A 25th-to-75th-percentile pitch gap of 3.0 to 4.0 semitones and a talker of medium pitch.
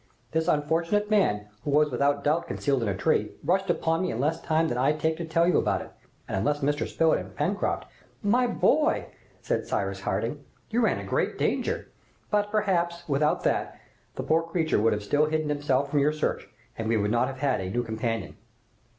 No: average, 4.4 semitones; medium, 150 Hz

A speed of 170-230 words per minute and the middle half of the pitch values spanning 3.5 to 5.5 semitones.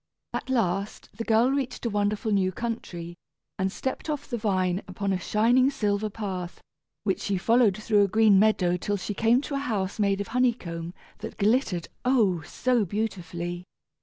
Yes: average, 175 wpm; average, 3.8 semitones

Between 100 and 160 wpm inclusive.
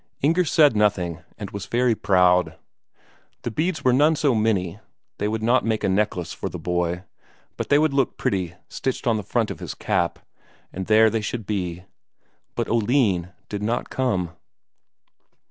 No: average, 170 wpm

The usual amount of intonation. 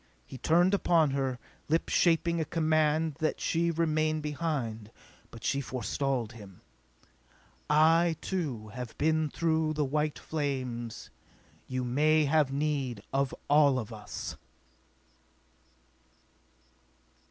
Yes: average, 3.6 semitones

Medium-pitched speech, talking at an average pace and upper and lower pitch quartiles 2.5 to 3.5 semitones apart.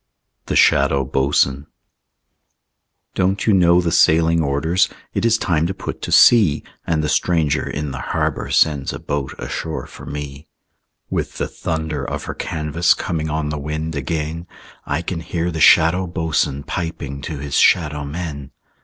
No: very low, 80 Hz; average, 160 wpm; average, 2.8 semitones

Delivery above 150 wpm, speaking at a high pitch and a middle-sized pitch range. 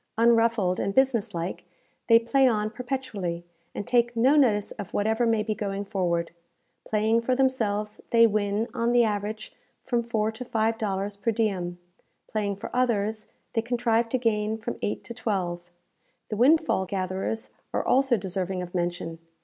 Yes: average, 160 wpm; high, 220 Hz; average, 3.0 semitones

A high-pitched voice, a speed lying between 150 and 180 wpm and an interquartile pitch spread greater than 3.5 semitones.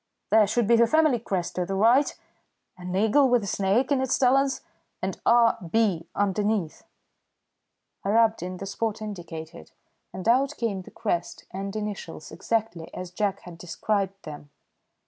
Yes: high, 205 Hz; average, 160 wpm; average, 4.0 semitones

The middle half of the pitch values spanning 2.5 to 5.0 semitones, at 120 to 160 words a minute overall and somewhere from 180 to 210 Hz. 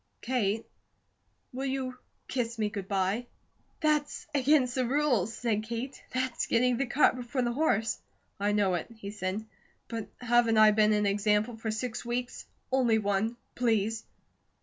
No: average, 3.1 semitones; average, 150 wpm; high, 230 Hz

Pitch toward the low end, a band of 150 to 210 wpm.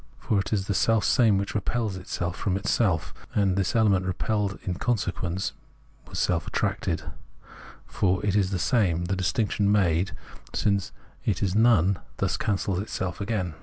Yes: very low, 95 Hz; average, 160 wpm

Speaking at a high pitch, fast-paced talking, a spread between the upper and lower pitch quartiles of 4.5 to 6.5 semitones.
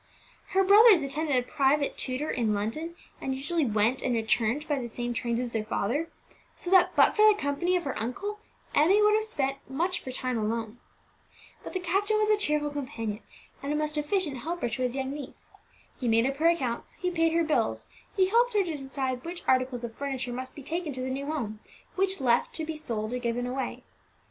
Yes: very high, 280 Hz; fast, 215 wpm; wide, 5.6 semitones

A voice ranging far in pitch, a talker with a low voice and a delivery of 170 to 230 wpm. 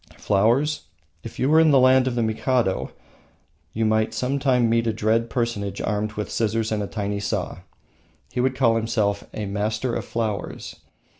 No: average, 3.1 semitones; low, 115 Hz; average, 175 wpm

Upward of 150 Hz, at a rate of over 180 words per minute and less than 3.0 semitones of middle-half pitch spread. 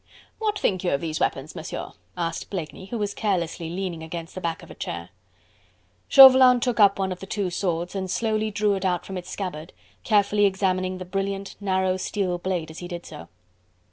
Yes: high, 190 Hz; average, 200 wpm; narrow, 2.6 semitones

